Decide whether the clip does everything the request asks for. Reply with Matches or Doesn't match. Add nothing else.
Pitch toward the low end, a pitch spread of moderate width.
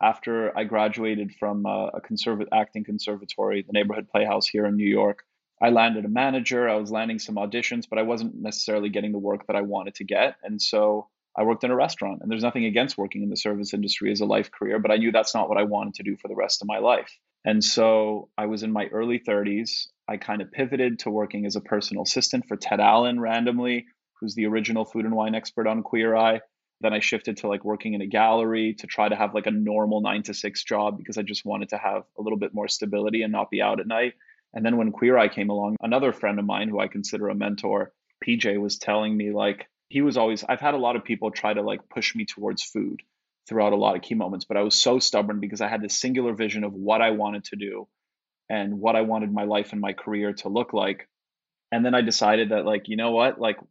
Doesn't match